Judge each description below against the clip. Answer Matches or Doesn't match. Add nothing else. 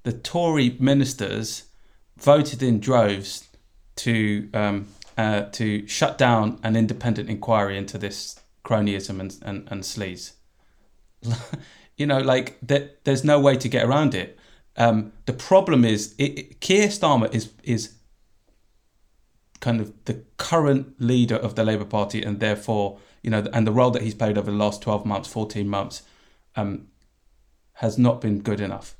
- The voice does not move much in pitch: Doesn't match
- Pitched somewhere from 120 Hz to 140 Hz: Doesn't match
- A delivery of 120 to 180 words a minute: Matches